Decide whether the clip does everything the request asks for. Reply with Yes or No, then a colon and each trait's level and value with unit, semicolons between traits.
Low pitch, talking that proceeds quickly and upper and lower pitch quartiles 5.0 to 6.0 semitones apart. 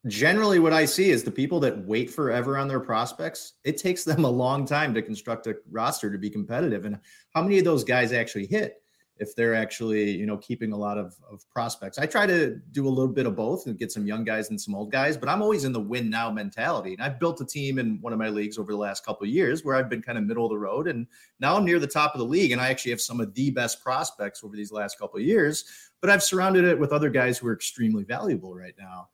Yes: low, 120 Hz; fast, 275 wpm; wide, 5.6 semitones